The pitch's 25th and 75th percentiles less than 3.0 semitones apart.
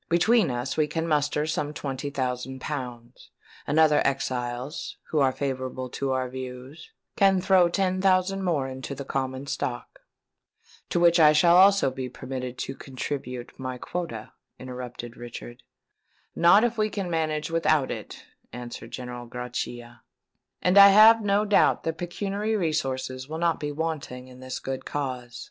No: average, 5.1 semitones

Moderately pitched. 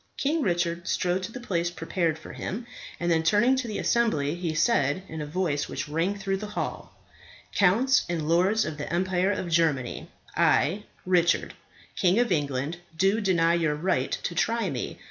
Yes: medium, 175 Hz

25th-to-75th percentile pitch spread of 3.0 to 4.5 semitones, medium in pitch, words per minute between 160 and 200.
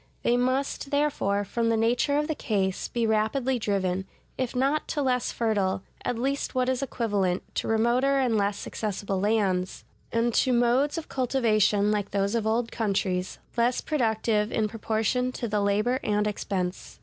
No: average, 3.6 semitones; high, 225 Hz; average, 165 wpm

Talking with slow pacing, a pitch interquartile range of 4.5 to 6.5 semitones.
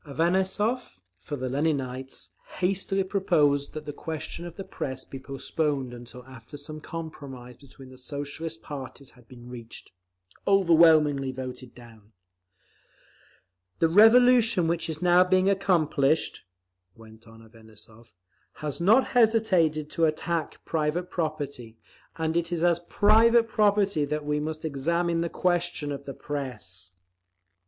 Yes: slow, 130 wpm; average, 4.9 semitones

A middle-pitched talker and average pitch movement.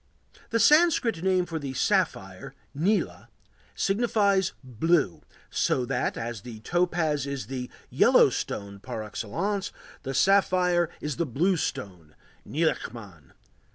No: medium, 160 Hz; wide, 7.9 semitones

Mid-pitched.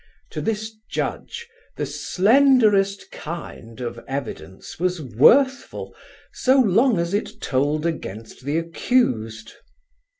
Yes: medium, 170 Hz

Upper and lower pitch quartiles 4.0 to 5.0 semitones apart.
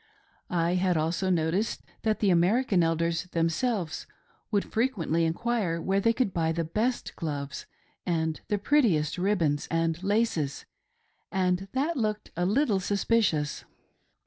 Yes: average, 4.4 semitones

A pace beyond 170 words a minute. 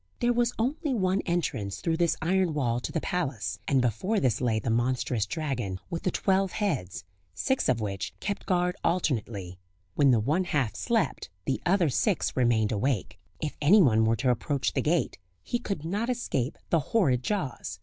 Yes: average, 180 wpm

